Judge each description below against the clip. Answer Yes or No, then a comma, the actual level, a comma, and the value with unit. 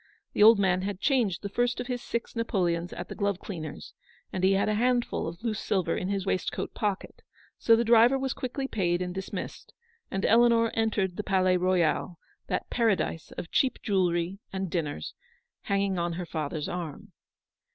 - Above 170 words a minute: Yes, average, 185 wpm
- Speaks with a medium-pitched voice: No, high, 195 Hz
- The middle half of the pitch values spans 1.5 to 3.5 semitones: No, average, 4.3 semitones